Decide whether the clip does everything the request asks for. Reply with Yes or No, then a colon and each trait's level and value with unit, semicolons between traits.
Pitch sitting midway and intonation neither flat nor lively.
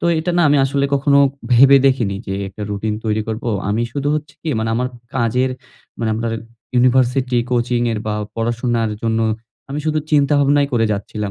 No: low, 120 Hz; average, 3.8 semitones